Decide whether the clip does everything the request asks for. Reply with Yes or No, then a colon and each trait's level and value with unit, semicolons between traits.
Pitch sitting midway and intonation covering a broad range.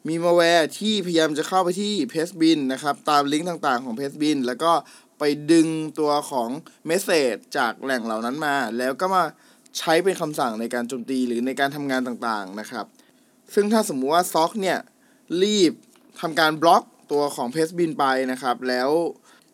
No: medium, 155 Hz; average, 4.6 semitones